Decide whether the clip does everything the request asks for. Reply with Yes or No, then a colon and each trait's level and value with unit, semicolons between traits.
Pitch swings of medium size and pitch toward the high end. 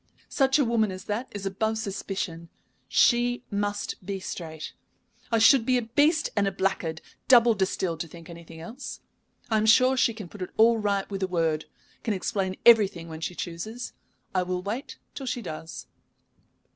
Yes: average, 4.6 semitones; high, 200 Hz